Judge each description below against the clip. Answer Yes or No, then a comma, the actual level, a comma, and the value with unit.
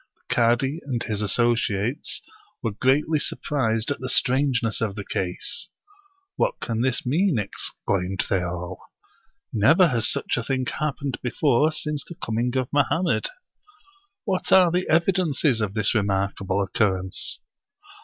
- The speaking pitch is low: Yes, low, 125 Hz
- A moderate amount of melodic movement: No, wide, 6.1 semitones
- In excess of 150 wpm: No, average, 145 wpm